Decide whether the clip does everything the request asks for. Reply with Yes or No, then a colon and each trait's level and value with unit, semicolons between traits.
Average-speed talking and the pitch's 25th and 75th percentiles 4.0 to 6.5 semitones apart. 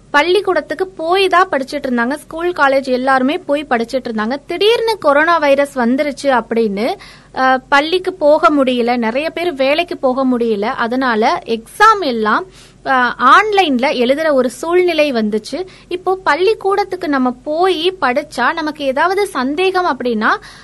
Yes: average, 120 wpm; wide, 5.6 semitones